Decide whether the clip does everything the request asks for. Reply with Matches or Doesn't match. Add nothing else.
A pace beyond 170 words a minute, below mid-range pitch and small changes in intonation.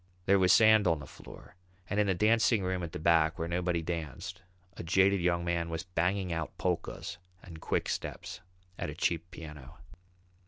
Matches